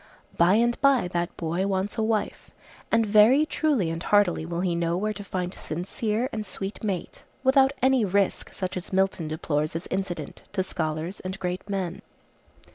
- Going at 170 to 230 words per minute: Yes, average, 180 wpm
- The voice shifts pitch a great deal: No, average, 3.7 semitones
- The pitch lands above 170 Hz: Yes, high, 190 Hz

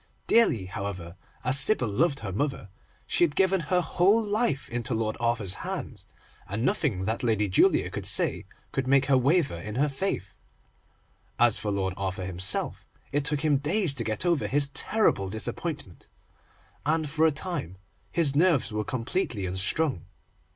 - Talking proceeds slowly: No, average, 160 wpm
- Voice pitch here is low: Yes, low, 130 Hz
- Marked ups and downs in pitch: Yes, wide, 7.5 semitones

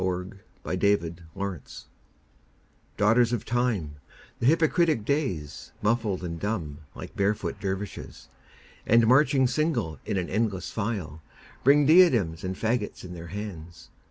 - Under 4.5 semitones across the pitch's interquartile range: No, average, 5.3 semitones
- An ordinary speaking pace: No, slow, 130 wpm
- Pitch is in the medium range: No, low, 105 Hz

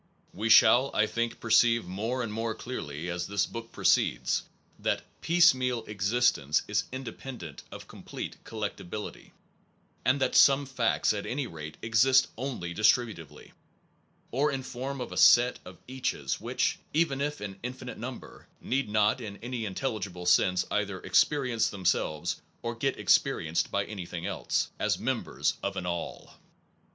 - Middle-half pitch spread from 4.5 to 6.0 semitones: Yes, average, 4.9 semitones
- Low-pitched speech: Yes, low, 115 Hz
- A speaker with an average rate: Yes, average, 145 wpm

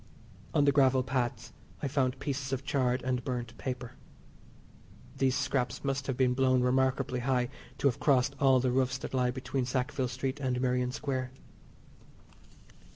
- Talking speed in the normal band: Yes, average, 160 wpm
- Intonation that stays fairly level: Yes, narrow, 1.3 semitones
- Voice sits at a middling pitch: No, low, 130 Hz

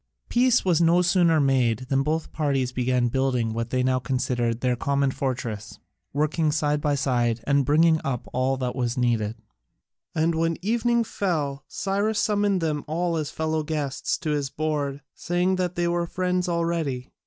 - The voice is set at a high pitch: No, medium, 150 Hz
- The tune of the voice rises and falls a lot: No, average, 4.8 semitones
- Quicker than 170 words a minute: No, average, 165 wpm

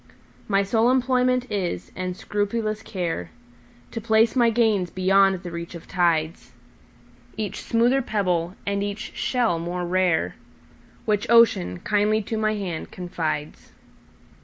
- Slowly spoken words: Yes, slow, 115 wpm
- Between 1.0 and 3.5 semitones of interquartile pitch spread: No, average, 4.5 semitones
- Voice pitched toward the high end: Yes, high, 195 Hz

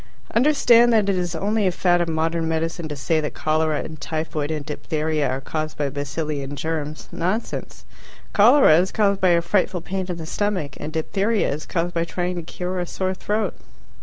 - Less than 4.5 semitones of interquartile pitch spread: Yes, average, 3.5 semitones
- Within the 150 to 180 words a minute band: No, average, 195 wpm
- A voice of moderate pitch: Yes, medium, 165 Hz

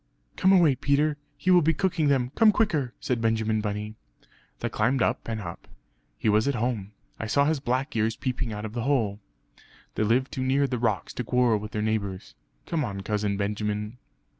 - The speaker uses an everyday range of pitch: Yes, average, 4.8 semitones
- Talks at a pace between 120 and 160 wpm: No, average, 195 wpm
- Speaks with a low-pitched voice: Yes, low, 120 Hz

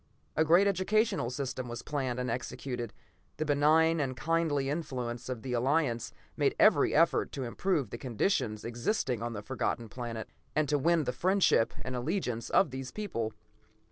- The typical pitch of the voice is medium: No, low, 130 Hz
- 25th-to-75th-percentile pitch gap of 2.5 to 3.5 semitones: No, average, 5.0 semitones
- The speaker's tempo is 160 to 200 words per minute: Yes, average, 165 wpm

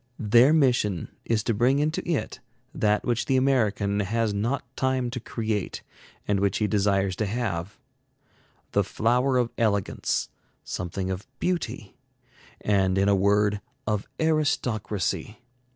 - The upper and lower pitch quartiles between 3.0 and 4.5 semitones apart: Yes, average, 3.7 semitones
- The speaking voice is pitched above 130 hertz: No, low, 110 Hz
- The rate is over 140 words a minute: No, slow, 135 wpm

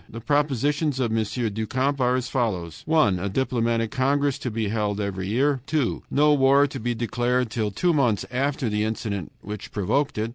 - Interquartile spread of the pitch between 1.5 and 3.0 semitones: No, average, 4.4 semitones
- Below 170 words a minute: No, average, 190 wpm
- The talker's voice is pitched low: Yes, low, 120 Hz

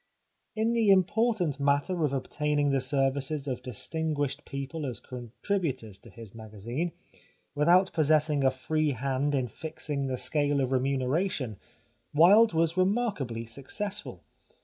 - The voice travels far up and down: No, average, 4.2 semitones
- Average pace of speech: No, slow, 125 wpm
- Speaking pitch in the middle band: Yes, medium, 145 Hz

